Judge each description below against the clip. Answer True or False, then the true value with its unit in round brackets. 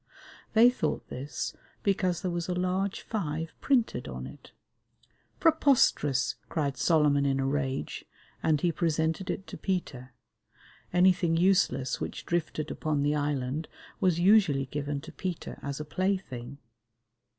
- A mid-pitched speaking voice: True (160 Hz)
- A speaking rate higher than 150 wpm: False (140 wpm)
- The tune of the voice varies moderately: True (4.7 semitones)